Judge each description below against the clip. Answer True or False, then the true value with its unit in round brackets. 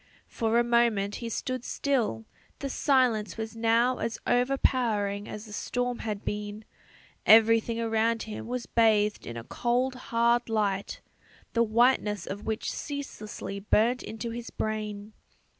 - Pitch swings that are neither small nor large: False (2.3 semitones)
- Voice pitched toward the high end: True (225 Hz)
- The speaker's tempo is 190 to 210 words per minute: False (140 wpm)